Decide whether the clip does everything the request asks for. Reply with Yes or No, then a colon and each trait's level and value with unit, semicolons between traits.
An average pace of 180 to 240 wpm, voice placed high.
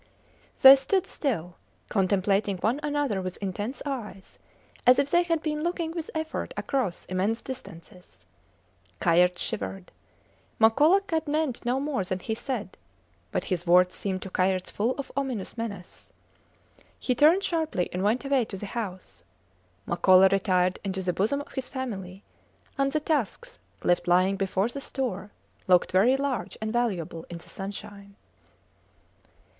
No: average, 150 wpm; high, 210 Hz